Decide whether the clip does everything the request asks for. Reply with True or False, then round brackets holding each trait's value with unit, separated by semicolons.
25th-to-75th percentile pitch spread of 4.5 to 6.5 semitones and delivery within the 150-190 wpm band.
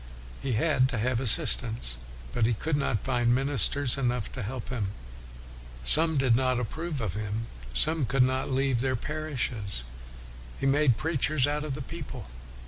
False (3.8 semitones; 160 wpm)